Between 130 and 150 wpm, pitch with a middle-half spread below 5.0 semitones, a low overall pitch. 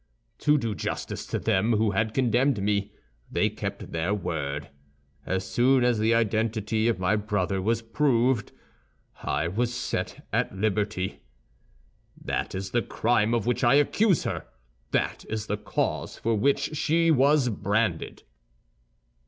Yes: average, 145 wpm; average, 3.3 semitones; low, 110 Hz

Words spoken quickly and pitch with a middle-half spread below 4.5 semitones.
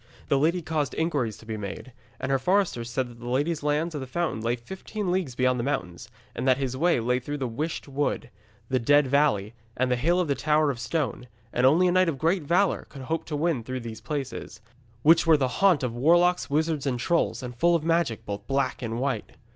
No: fast, 230 wpm; average, 4.9 semitones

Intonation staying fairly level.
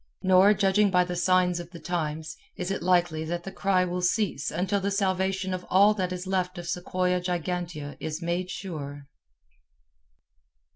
Yes: narrow, 1.6 semitones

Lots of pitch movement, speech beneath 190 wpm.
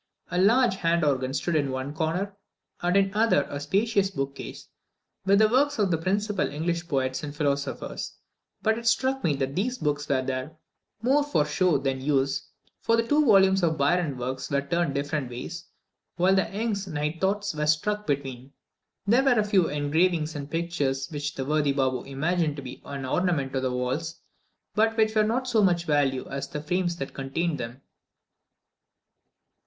Yes: wide, 6.0 semitones; average, 180 wpm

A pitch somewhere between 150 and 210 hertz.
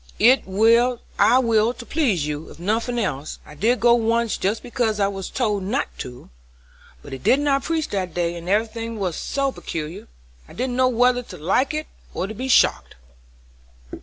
No: high, 225 Hz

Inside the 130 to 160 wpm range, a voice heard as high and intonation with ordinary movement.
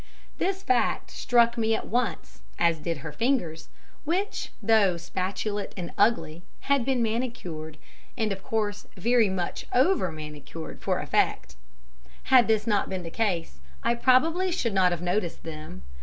No: average, 150 wpm; high, 210 Hz; wide, 6.0 semitones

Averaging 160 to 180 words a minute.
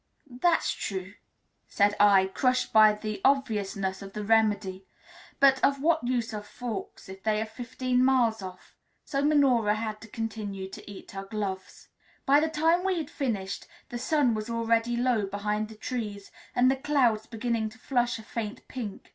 Yes: average, 170 wpm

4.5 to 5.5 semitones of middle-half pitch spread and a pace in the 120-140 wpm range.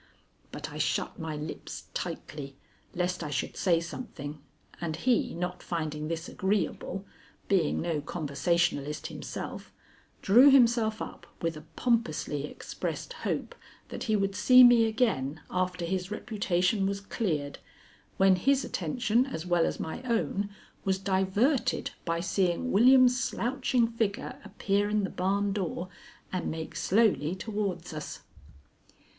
Yes: average, 4.9 semitones; slow, 135 wpm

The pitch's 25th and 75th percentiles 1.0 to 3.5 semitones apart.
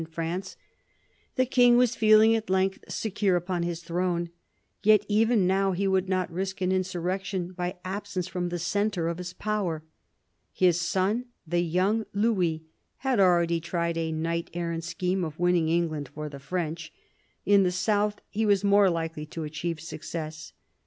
Yes: average, 3.0 semitones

